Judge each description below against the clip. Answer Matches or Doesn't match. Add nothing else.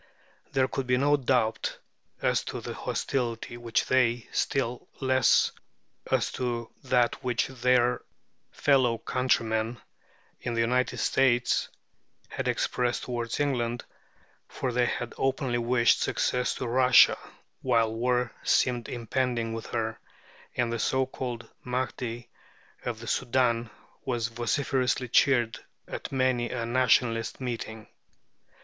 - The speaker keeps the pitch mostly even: Matches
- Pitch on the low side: Matches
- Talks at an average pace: Doesn't match